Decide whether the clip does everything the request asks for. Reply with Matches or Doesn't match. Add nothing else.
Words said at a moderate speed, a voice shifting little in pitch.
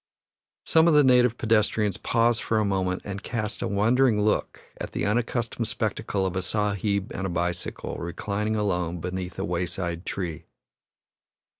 Doesn't match